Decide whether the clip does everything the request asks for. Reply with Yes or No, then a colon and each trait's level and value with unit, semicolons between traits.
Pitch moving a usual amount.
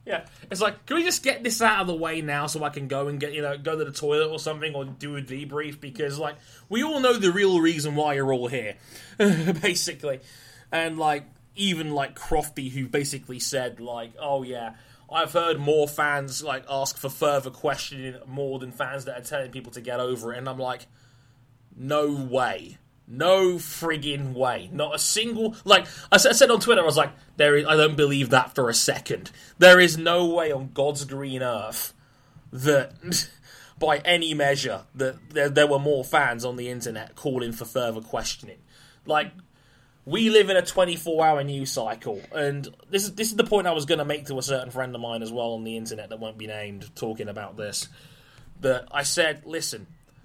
Yes: average, 3.6 semitones